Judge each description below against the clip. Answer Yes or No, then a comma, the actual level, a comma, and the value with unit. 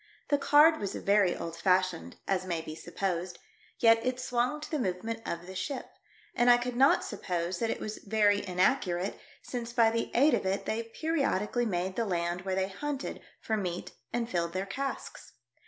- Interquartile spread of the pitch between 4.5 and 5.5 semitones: Yes, average, 4.8 semitones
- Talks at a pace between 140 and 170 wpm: No, average, 190 wpm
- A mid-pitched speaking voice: No, high, 205 Hz